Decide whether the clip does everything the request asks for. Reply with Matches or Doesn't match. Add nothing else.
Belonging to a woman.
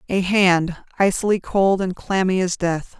Matches